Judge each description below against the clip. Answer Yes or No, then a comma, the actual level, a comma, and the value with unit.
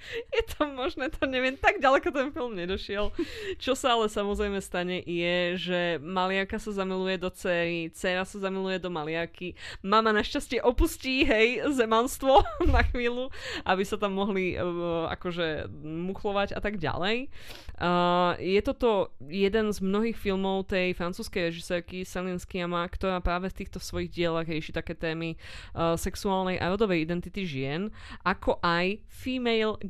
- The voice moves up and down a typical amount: Yes, average, 4.2 semitones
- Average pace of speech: Yes, average, 150 wpm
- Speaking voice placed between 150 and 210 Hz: Yes, high, 190 Hz